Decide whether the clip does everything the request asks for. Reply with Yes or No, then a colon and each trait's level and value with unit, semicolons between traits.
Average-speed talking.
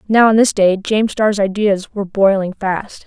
Yes: average, 195 wpm